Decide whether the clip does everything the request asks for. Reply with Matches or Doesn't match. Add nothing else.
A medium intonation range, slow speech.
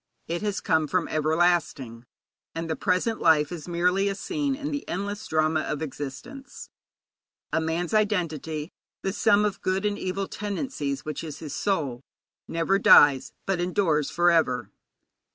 Doesn't match